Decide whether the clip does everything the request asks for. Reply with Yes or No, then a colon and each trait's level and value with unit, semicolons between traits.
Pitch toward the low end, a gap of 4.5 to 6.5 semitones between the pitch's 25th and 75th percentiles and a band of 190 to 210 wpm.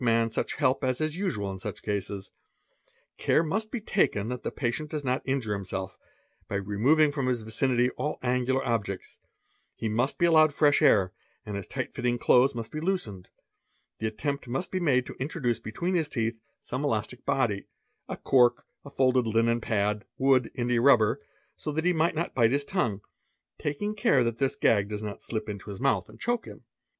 Yes: low, 125 Hz; average, 5.0 semitones; average, 195 wpm